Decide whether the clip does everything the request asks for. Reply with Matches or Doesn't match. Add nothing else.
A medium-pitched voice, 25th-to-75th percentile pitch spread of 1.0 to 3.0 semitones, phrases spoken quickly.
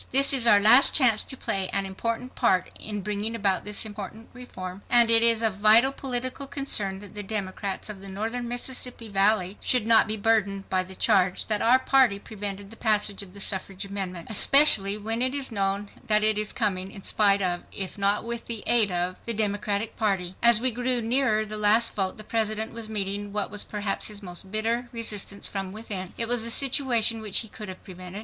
Doesn't match